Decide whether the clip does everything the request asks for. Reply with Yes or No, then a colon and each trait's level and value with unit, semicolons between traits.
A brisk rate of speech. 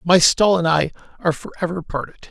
Yes: fast, 210 wpm